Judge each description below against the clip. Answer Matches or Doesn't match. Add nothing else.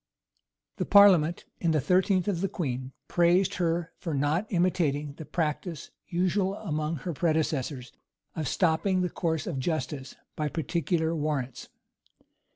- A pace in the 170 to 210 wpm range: Doesn't match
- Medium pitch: Matches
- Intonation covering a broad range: Doesn't match